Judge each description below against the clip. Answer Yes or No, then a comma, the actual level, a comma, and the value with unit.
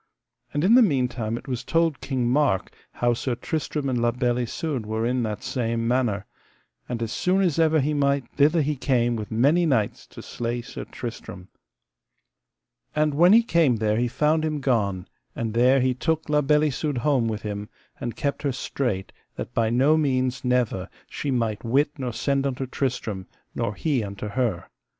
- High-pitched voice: No, low, 125 Hz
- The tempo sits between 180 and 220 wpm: Yes, average, 185 wpm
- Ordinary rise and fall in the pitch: Yes, average, 4.2 semitones